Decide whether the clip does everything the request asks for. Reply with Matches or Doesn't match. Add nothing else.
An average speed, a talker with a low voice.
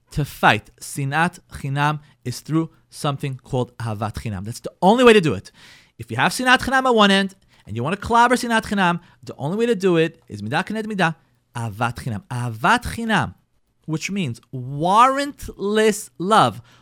Doesn't match